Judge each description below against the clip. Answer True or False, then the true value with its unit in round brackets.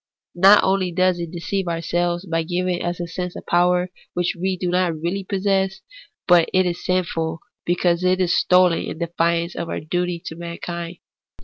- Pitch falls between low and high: True (175 Hz)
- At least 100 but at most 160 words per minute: False (180 wpm)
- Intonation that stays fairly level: True (1.4 semitones)